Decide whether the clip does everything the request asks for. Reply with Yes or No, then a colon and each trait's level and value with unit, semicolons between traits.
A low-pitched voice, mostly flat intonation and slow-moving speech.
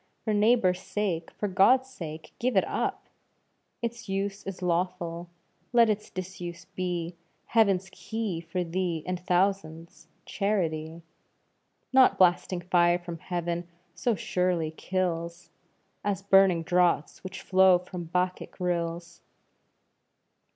No: medium, 180 Hz; narrow, 2.3 semitones; slow, 115 wpm